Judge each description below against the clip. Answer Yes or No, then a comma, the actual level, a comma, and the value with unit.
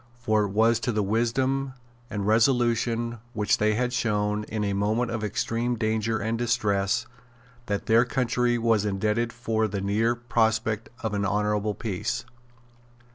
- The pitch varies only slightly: Yes, narrow, 2.1 semitones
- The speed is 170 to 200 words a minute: No, average, 150 wpm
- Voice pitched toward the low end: Yes, low, 110 Hz